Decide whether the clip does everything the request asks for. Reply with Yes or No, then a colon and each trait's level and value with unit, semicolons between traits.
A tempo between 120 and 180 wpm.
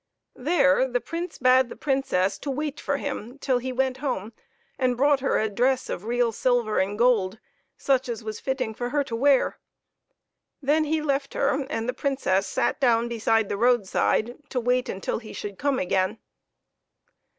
Yes: average, 175 wpm